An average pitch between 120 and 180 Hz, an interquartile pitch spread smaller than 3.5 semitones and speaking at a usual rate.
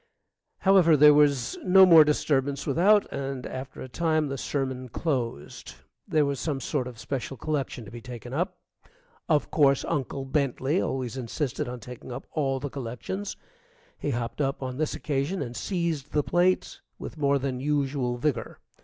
Yes: medium, 140 Hz; average, 3.0 semitones; average, 170 wpm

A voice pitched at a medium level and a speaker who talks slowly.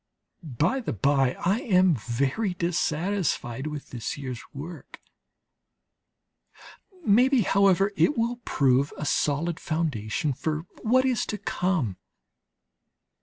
Yes: medium, 165 Hz; slow, 110 wpm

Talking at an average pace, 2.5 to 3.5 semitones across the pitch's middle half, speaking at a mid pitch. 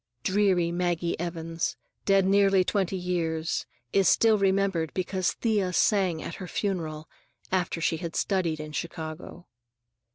No: slow, 130 wpm; average, 2.8 semitones; medium, 180 Hz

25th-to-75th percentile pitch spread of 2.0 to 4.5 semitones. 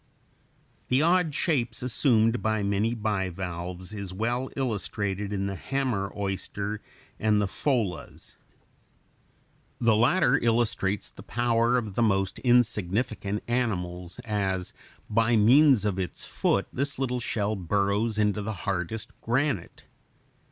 Yes: average, 3.5 semitones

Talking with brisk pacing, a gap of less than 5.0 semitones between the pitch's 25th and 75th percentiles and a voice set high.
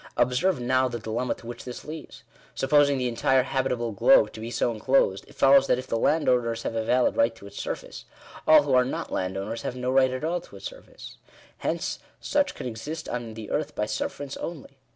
No: fast, 215 wpm; average, 3.4 semitones; low, 125 Hz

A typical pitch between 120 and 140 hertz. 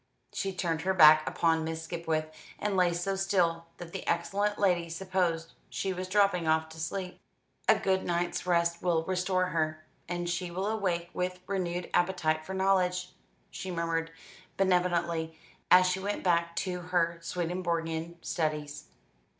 No: medium, 175 Hz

